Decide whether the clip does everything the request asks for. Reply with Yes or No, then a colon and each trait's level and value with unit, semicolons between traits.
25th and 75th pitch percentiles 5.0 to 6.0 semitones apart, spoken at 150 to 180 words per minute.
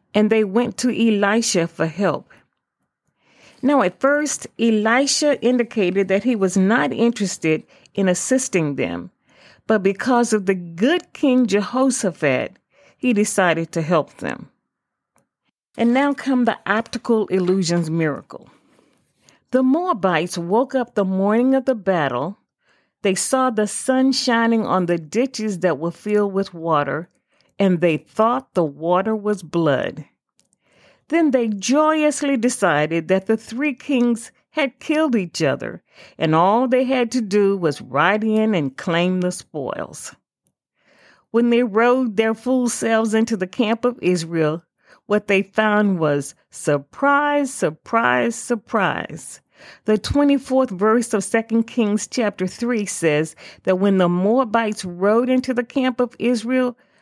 No: average, 5.3 semitones; average, 140 wpm